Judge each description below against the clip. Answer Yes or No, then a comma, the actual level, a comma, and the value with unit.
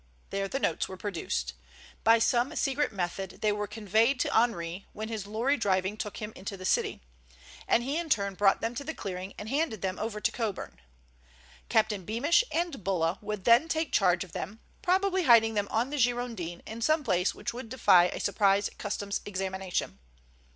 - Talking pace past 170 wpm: Yes, average, 185 wpm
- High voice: Yes, high, 215 Hz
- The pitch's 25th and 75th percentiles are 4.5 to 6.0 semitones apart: No, average, 4.1 semitones